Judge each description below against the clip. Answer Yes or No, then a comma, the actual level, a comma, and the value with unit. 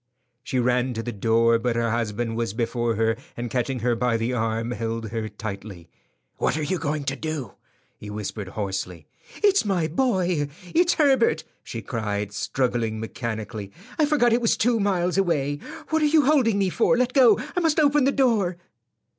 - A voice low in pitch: Yes, low, 125 Hz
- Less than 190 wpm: Yes, average, 180 wpm